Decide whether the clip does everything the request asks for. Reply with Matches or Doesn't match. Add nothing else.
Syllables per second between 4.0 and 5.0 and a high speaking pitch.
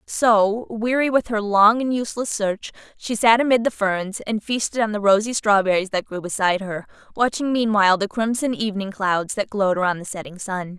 Doesn't match